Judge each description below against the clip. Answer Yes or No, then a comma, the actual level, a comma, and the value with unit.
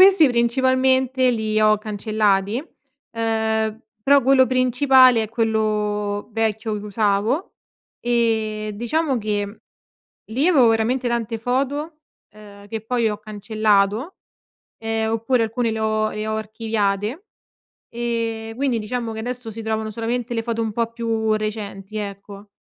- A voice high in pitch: Yes, high, 225 Hz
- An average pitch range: No, narrow, 2.3 semitones